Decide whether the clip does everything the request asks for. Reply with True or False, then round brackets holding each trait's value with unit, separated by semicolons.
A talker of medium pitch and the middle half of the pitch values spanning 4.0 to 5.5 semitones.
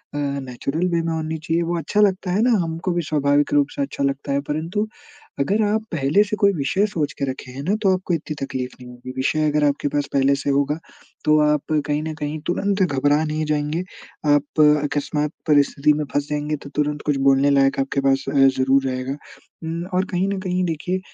False (150 Hz; 3.4 semitones)